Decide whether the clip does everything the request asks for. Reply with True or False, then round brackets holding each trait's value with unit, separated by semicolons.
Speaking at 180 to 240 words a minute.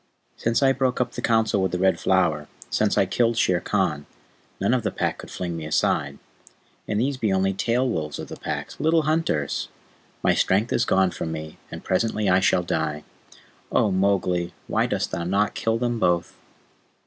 True (190 wpm)